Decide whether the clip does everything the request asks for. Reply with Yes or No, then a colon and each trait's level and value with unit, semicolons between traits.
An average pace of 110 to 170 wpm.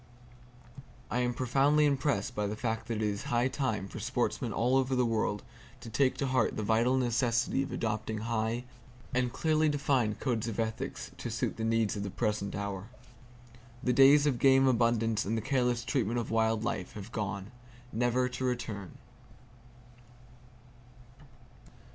Yes: average, 165 wpm